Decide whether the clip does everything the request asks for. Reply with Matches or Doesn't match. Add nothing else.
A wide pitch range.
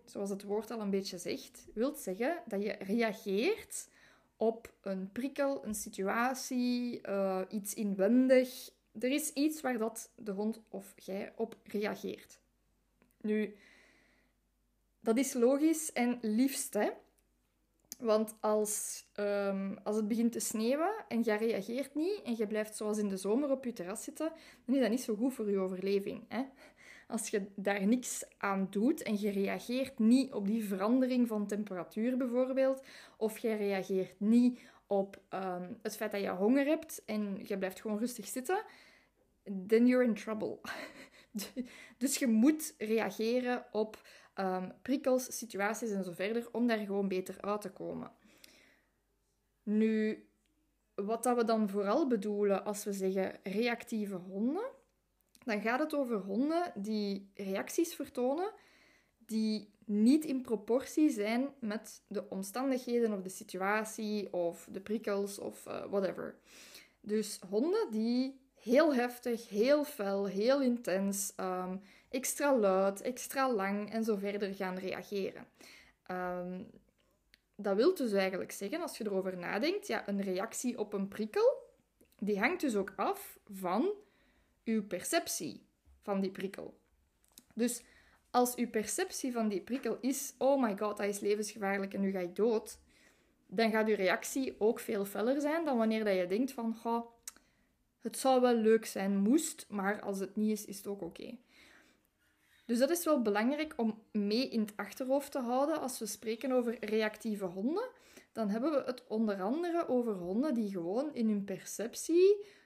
Doesn't match